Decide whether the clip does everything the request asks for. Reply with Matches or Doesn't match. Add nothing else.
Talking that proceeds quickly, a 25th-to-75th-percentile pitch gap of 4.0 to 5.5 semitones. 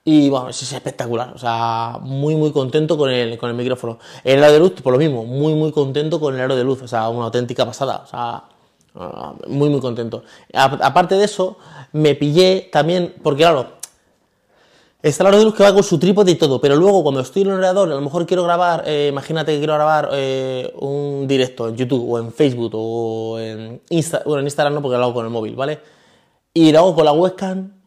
Matches